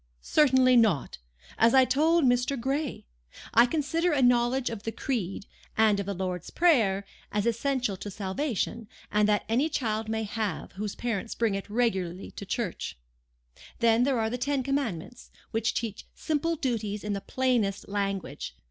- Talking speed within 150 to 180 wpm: Yes, average, 160 wpm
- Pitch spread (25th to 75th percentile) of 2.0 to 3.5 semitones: No, average, 4.3 semitones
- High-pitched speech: Yes, high, 230 Hz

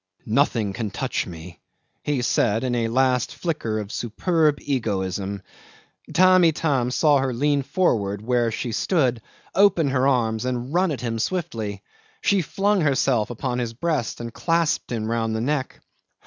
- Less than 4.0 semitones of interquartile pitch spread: No, average, 4.9 semitones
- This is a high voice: No, low, 125 Hz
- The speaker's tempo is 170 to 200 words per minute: No, average, 155 wpm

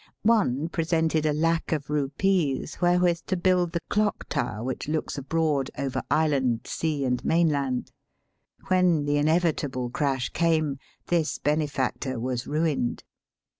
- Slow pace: Yes, slow, 130 wpm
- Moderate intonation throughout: Yes, average, 3.7 semitones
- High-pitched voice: No, medium, 150 Hz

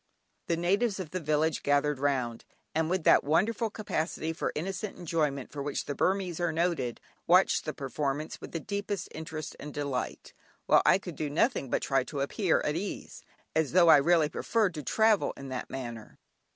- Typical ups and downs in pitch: Yes, average, 4.4 semitones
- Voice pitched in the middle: Yes, medium, 160 Hz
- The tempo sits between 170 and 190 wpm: Yes, average, 185 wpm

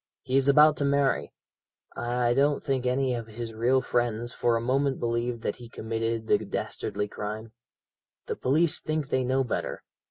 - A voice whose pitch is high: No, low, 125 Hz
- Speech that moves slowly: No, average, 170 wpm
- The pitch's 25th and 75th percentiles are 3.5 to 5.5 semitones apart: No, average, 2.8 semitones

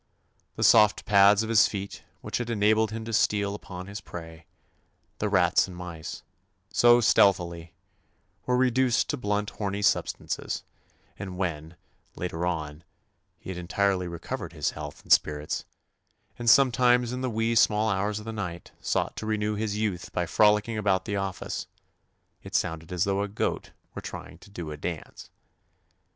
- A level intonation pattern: No, average, 3.7 semitones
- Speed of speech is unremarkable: Yes, average, 165 wpm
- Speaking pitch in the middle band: No, low, 100 Hz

